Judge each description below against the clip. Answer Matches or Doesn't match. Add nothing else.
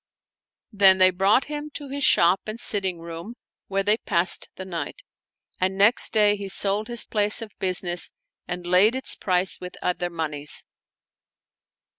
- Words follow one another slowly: Doesn't match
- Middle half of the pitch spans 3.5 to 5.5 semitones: Doesn't match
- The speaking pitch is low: Doesn't match